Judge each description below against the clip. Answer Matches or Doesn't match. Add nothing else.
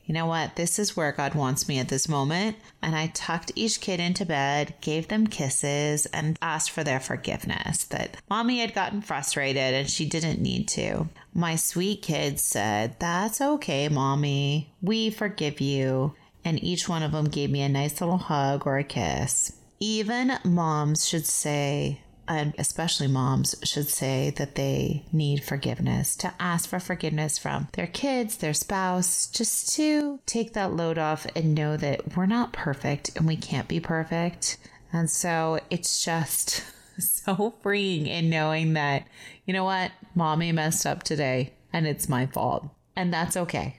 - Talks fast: Doesn't match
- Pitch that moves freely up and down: Doesn't match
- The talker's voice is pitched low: Doesn't match